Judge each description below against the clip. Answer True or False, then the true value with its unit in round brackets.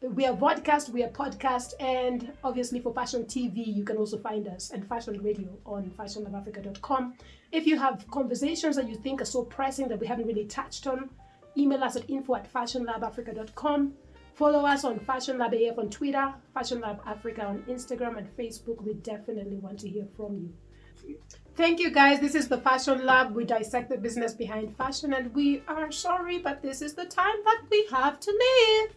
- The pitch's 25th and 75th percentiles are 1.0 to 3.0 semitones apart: False (3.7 semitones)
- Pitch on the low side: False (255 Hz)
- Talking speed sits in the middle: True (195 wpm)